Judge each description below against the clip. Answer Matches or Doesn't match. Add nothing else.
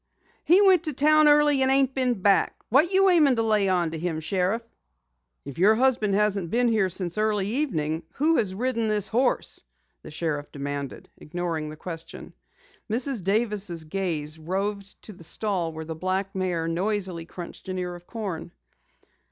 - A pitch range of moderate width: Doesn't match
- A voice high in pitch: Matches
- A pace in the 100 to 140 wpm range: Doesn't match